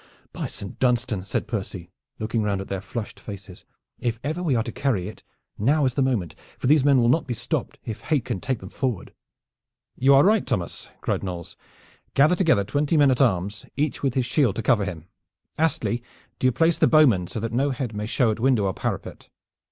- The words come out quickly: Yes, fast, 215 wpm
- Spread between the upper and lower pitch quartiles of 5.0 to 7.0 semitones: Yes, average, 5.3 semitones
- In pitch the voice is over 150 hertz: No, low, 120 Hz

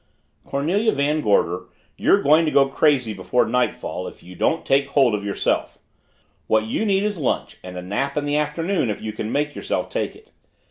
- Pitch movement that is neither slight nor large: No, wide, 6.0 semitones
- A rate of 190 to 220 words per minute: Yes, average, 195 wpm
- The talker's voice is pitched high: No, medium, 140 Hz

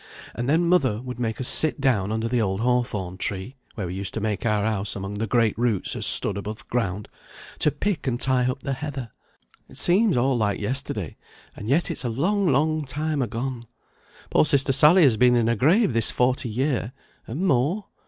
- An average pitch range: Yes, average, 4.5 semitones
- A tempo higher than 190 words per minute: Yes, fast, 205 wpm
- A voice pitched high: No, low, 125 Hz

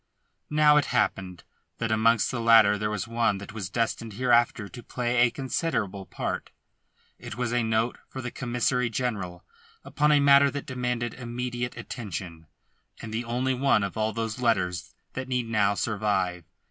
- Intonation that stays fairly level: No, average, 3.2 semitones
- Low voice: Yes, low, 115 Hz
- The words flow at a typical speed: Yes, average, 165 wpm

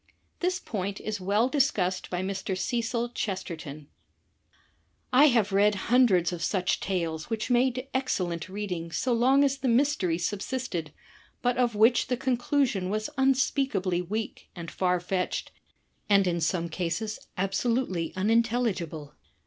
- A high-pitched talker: Yes, high, 205 Hz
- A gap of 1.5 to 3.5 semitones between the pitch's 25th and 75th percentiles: No, wide, 5.4 semitones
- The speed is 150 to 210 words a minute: No, slow, 135 wpm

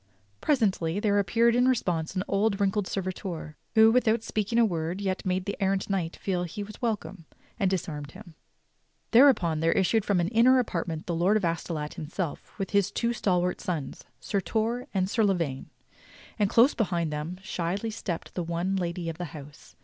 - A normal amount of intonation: Yes, average, 4.2 semitones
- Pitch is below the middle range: No, high, 190 Hz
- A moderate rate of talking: Yes, average, 195 wpm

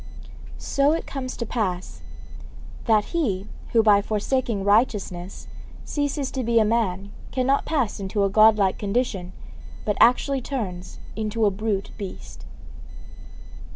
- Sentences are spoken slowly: Yes, slow, 125 wpm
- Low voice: No, high, 215 Hz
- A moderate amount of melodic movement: Yes, average, 4.3 semitones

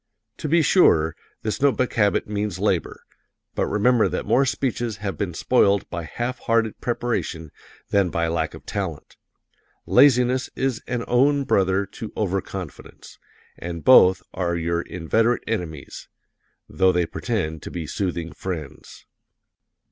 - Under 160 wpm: Yes, average, 140 wpm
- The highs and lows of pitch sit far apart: Yes, wide, 5.9 semitones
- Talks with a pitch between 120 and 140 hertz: No, low, 100 Hz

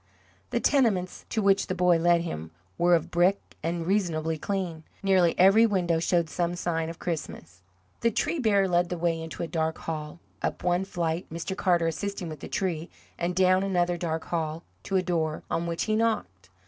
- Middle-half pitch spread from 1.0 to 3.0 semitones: Yes, narrow, 2.6 semitones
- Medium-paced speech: Yes, average, 190 wpm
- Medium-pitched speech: Yes, medium, 175 Hz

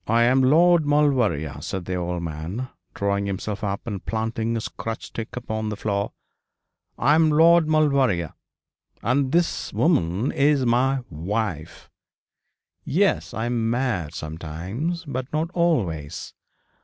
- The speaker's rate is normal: No, slow, 130 wpm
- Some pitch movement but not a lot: No, wide, 7.2 semitones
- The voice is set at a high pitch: No, low, 115 Hz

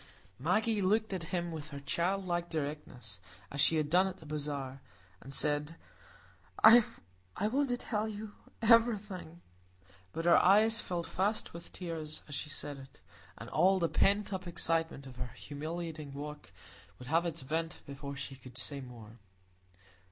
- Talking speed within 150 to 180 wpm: Yes, average, 160 wpm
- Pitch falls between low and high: Yes, medium, 165 Hz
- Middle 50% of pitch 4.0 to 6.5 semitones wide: Yes, average, 5.1 semitones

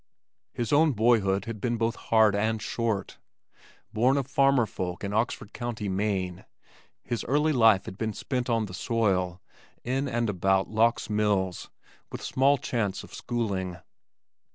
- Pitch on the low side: Yes, low, 110 Hz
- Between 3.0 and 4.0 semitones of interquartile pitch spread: Yes, average, 3.6 semitones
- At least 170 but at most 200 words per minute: No, average, 150 wpm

